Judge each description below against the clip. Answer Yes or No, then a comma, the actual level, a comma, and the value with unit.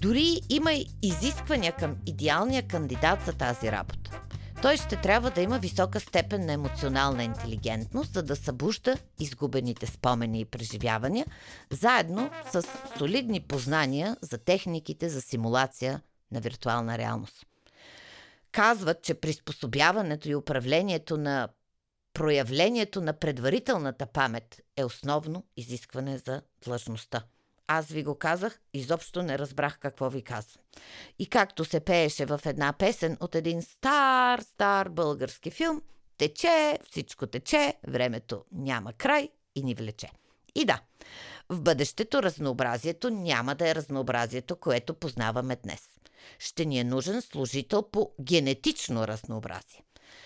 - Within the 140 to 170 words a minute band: No, average, 125 wpm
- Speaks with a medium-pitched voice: Yes, medium, 145 Hz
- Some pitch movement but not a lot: No, wide, 6.8 semitones